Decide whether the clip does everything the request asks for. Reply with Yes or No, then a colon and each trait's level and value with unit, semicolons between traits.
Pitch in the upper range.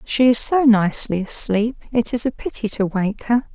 Yes: high, 225 Hz